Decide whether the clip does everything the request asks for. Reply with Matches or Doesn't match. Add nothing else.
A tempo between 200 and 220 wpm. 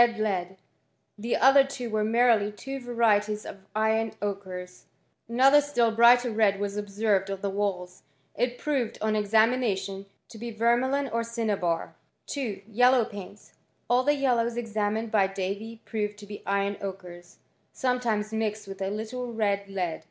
Doesn't match